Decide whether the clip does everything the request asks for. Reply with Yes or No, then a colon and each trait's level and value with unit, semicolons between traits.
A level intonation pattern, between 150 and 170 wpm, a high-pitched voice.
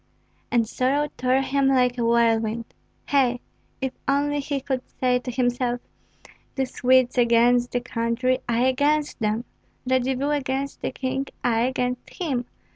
No: narrow, 1.8 semitones; average, 140 wpm; very high, 255 Hz